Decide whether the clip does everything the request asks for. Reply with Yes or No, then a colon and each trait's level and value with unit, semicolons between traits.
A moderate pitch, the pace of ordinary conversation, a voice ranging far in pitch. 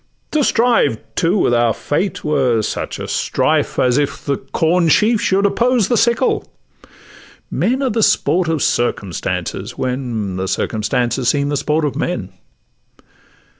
Yes: medium, 145 Hz; average, 145 wpm; wide, 8.9 semitones